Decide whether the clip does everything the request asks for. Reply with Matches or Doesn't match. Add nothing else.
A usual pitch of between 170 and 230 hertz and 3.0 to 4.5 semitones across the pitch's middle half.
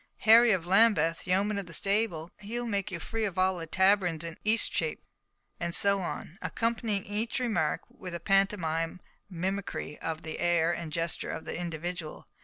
Matches